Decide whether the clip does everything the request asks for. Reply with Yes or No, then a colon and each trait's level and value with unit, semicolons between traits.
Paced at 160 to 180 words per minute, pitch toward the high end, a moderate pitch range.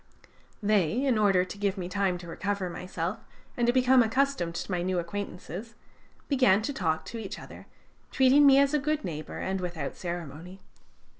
No: average, 175 wpm; high, 195 Hz; wide, 6.0 semitones